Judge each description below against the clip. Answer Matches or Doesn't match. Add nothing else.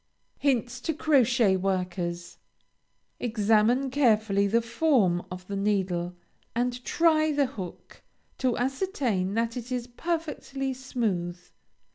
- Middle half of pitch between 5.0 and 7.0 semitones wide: Matches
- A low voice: Doesn't match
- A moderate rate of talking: Doesn't match